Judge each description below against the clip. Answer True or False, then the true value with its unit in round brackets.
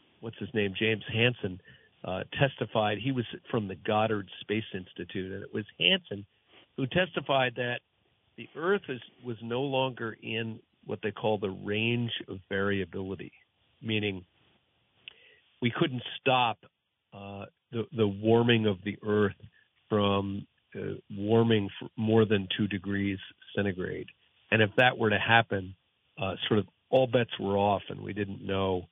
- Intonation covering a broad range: False (2.9 semitones)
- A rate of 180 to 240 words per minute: False (145 wpm)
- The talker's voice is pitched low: True (110 Hz)